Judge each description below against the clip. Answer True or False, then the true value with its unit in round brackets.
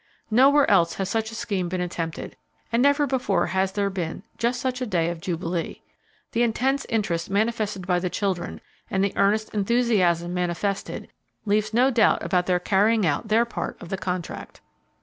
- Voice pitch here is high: True (200 Hz)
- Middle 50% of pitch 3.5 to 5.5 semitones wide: True (4.4 semitones)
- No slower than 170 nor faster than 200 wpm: True (175 wpm)